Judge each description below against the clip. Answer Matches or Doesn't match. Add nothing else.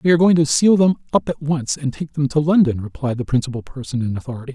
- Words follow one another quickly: Matches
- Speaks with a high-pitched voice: Doesn't match